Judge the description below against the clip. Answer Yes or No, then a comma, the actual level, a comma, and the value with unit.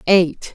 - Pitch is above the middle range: No, medium, 175 Hz